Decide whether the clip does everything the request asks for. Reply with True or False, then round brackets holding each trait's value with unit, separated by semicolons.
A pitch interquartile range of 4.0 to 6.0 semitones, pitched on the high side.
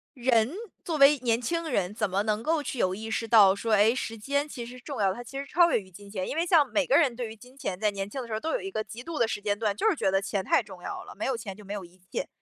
True (5.3 semitones; 230 Hz)